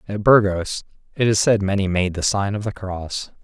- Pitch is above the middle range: No, low, 100 Hz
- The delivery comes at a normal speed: No, fast, 210 wpm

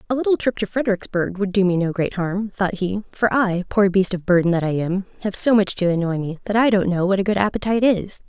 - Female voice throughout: Yes, female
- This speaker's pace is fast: Yes, fast, 270 wpm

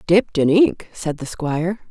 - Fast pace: No, average, 190 wpm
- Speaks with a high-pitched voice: No, medium, 175 Hz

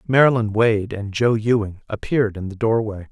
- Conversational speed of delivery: Yes, average, 175 wpm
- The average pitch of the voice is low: Yes, low, 110 Hz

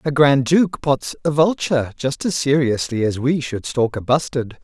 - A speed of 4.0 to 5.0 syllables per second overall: Yes, 4.6 syllables/s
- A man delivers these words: Yes, male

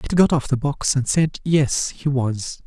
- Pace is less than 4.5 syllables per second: Yes, 4.2 syllables/s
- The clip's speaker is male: Yes, male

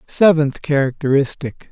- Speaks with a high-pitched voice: No, medium, 145 Hz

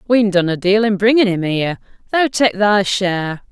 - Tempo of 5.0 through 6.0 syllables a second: Yes, 5.1 syllables/s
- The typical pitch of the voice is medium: No, high, 200 Hz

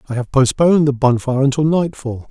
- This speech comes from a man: Yes, male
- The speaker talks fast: No, average, 185 wpm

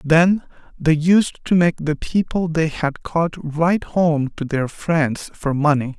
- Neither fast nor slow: Yes, average, 170 wpm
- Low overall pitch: No, medium, 160 Hz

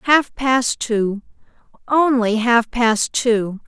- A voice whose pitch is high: Yes, high, 235 Hz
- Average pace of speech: No, slow, 100 wpm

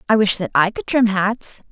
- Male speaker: No, female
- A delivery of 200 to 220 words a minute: No, fast, 245 wpm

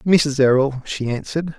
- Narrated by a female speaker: No, male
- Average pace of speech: Yes, average, 150 wpm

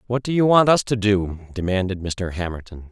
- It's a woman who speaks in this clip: No, male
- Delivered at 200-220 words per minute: Yes, fast, 205 wpm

